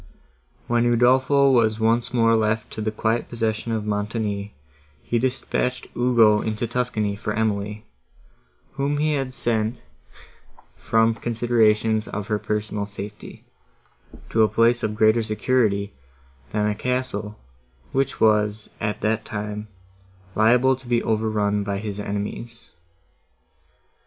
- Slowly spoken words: Yes, slow, 125 wpm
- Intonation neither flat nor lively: No, narrow, 2.1 semitones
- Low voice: Yes, low, 110 Hz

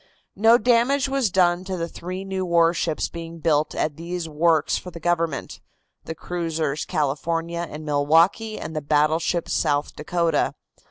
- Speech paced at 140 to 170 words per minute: Yes, average, 150 wpm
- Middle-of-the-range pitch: Yes, medium, 170 Hz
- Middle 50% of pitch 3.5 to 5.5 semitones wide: No, narrow, 2.6 semitones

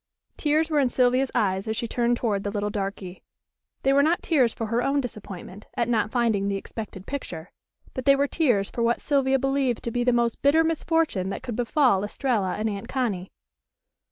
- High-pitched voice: Yes, high, 240 Hz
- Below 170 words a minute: No, average, 200 wpm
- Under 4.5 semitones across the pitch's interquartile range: No, average, 4.9 semitones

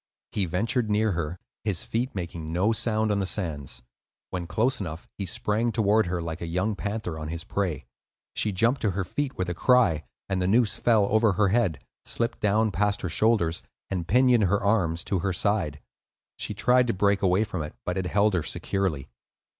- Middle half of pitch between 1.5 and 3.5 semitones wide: No, average, 4.0 semitones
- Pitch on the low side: Yes, low, 100 Hz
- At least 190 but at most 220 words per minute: Yes, average, 200 wpm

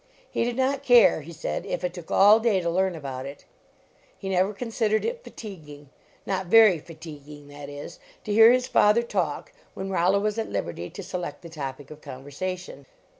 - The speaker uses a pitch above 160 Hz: Yes, medium, 185 Hz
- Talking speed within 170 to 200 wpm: Yes, average, 185 wpm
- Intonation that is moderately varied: No, wide, 6.4 semitones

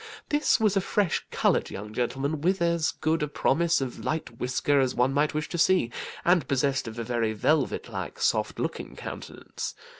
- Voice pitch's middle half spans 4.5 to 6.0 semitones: Yes, average, 5.2 semitones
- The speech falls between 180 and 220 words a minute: Yes, average, 185 wpm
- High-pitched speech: No, medium, 145 Hz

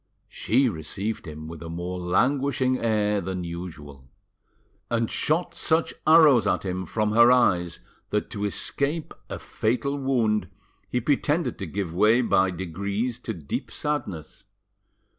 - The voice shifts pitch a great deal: Yes, wide, 6.3 semitones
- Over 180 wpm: No, average, 140 wpm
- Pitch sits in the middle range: No, low, 105 Hz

